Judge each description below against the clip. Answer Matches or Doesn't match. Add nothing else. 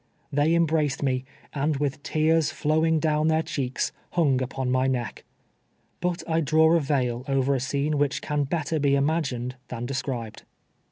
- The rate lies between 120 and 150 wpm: Doesn't match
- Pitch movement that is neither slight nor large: Matches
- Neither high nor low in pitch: Matches